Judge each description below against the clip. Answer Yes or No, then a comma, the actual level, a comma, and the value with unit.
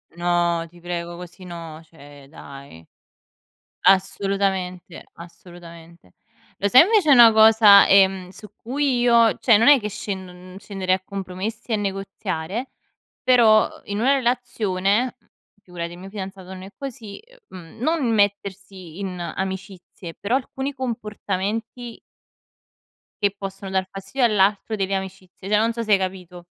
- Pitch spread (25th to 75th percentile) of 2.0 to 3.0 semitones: No, average, 3.6 semitones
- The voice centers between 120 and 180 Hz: No, high, 195 Hz